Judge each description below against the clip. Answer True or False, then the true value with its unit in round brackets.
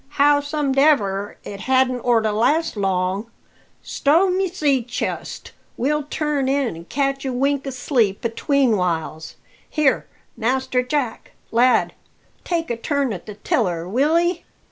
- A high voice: True (260 Hz)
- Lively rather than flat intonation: False (4.7 semitones)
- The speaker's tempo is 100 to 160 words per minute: True (140 wpm)